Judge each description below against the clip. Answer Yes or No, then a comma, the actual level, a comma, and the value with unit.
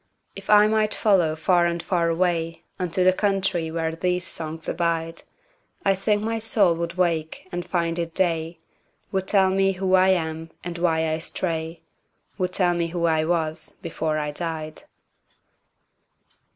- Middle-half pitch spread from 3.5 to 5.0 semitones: No, narrow, 2.5 semitones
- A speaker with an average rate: Yes, average, 145 wpm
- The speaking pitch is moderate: Yes, medium, 170 Hz